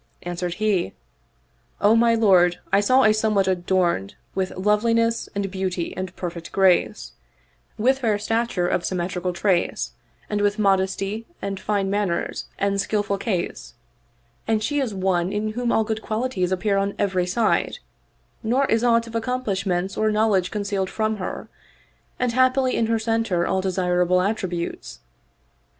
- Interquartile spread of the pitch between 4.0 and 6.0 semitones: No, average, 3.2 semitones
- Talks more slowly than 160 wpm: Yes, average, 150 wpm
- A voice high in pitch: Yes, high, 200 Hz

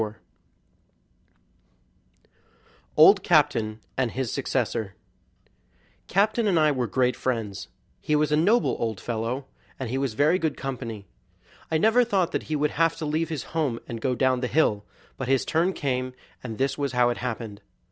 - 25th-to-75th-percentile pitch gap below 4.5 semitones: No, average, 5.1 semitones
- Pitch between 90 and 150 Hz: Yes, low, 135 Hz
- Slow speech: No, average, 165 wpm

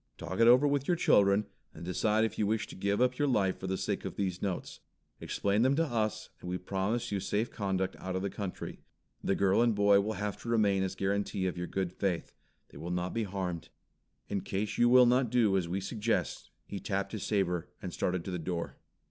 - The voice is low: Yes, low, 100 Hz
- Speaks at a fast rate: Yes, fast, 235 wpm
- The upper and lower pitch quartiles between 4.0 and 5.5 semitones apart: No, average, 2.9 semitones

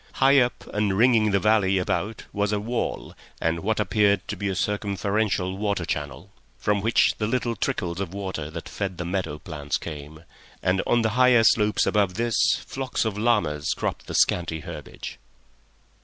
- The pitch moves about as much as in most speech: Yes, average, 3.6 semitones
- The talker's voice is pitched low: Yes, low, 100 Hz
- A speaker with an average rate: Yes, average, 170 wpm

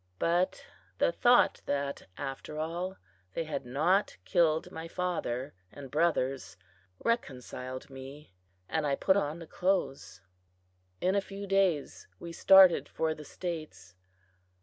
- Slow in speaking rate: Yes, slow, 125 wpm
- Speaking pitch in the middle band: Yes, medium, 160 Hz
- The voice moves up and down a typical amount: Yes, average, 4.9 semitones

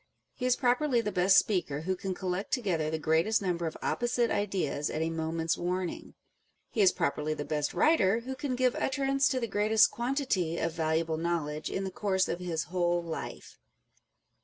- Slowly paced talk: No, average, 185 wpm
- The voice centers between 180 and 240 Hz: Yes, medium, 185 Hz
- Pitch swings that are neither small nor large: No, wide, 6.2 semitones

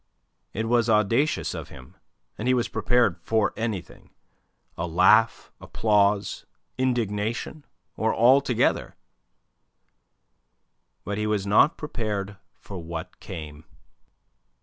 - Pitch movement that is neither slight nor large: Yes, average, 3.3 semitones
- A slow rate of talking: Yes, slow, 105 wpm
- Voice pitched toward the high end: No, low, 105 Hz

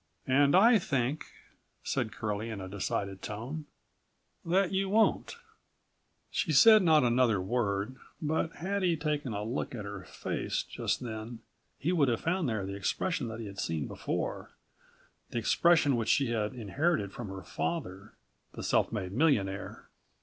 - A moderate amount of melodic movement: No, wide, 7.6 semitones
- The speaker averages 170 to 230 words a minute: No, average, 160 wpm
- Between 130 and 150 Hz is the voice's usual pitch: No, low, 120 Hz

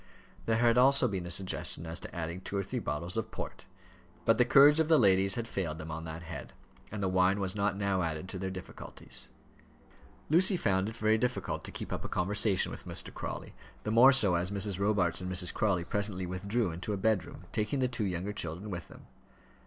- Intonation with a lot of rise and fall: No, average, 3.6 semitones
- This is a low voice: Yes, low, 100 Hz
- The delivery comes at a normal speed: No, fast, 215 wpm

